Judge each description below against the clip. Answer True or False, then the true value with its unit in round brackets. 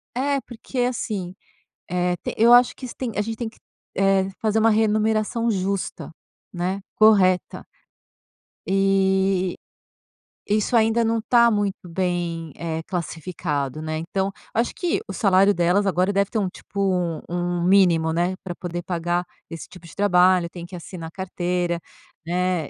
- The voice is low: False (190 Hz)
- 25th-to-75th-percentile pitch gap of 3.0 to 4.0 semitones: True (3.4 semitones)